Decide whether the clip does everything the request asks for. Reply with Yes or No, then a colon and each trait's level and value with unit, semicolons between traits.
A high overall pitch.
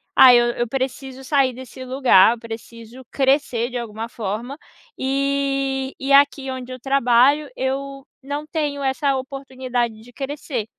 Yes: very high, 265 Hz